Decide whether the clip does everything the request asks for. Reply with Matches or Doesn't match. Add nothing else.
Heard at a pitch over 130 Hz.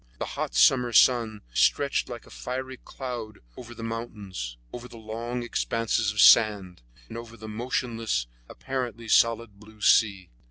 Doesn't match